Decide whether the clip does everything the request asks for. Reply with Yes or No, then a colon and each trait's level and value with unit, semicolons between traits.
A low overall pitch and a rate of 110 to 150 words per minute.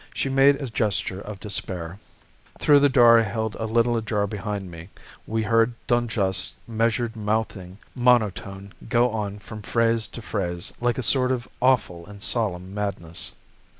No: low, 110 Hz; average, 160 wpm